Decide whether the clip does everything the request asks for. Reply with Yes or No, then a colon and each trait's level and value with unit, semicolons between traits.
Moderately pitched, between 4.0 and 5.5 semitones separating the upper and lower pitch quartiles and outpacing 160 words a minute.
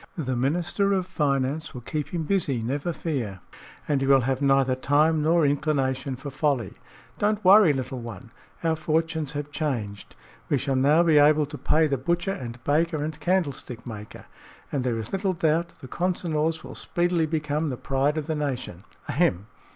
No: medium, 150 Hz; average, 3.5 semitones; average, 175 wpm